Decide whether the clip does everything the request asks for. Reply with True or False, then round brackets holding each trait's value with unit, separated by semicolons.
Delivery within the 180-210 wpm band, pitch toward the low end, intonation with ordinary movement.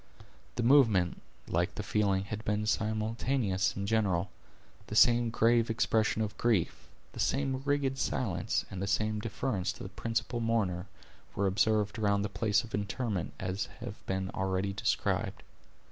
False (150 wpm; 105 Hz; 3.1 semitones)